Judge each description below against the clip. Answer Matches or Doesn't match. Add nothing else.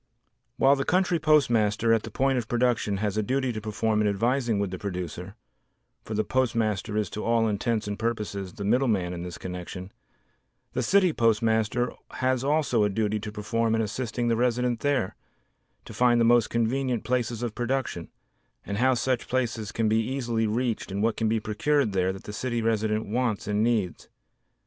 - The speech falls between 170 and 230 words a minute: Matches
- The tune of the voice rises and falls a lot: Doesn't match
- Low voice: Matches